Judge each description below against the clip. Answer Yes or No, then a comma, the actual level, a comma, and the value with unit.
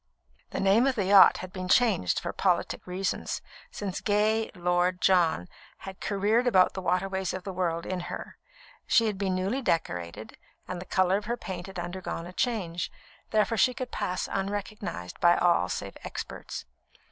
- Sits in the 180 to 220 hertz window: Yes, high, 190 Hz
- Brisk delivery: No, average, 170 wpm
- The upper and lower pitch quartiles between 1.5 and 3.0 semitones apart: Yes, narrow, 2.6 semitones